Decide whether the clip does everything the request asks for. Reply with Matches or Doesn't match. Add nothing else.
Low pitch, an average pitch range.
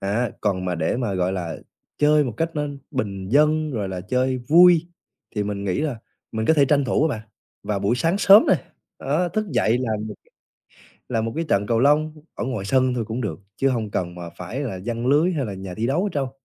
Doesn't match